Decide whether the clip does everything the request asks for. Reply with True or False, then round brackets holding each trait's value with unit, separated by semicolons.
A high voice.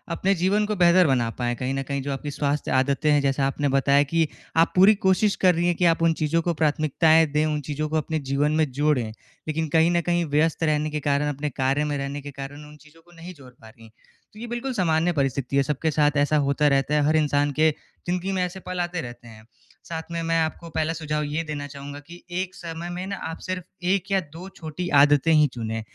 False (155 Hz)